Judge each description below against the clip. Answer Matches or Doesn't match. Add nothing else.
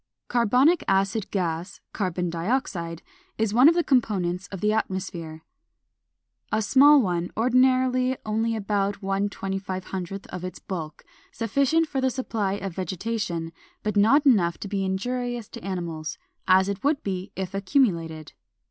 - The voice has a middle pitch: Doesn't match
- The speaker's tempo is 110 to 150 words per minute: Matches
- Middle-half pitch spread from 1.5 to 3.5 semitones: Doesn't match